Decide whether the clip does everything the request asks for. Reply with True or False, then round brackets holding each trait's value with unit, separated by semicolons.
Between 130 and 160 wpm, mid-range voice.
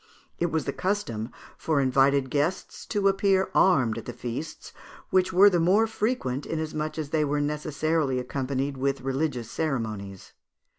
True (150 wpm; 150 Hz)